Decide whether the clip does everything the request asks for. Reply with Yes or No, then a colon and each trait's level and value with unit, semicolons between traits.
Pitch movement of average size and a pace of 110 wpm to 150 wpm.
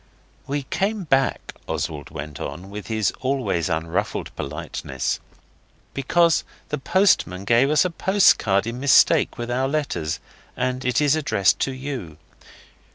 No: wide, 7.9 semitones; slow, 135 wpm